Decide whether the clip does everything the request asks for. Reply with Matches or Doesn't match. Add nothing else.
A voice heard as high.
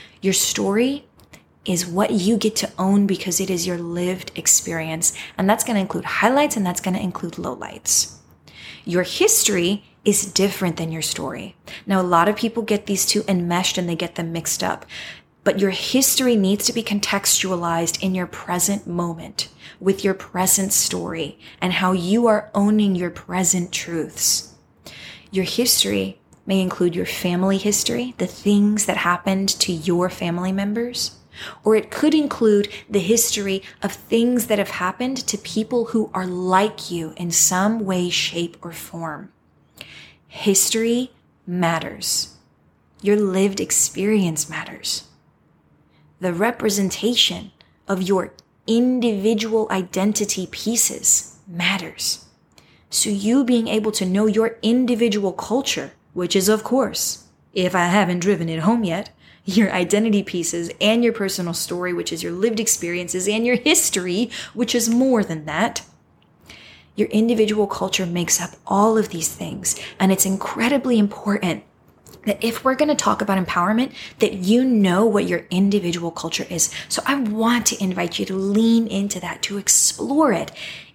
Matches